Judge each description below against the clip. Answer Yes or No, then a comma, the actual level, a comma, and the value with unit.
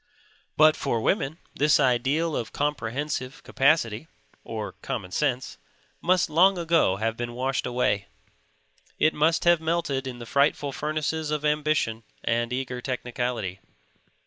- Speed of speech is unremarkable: No, slow, 130 wpm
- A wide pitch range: No, average, 4.2 semitones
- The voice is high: No, medium, 140 Hz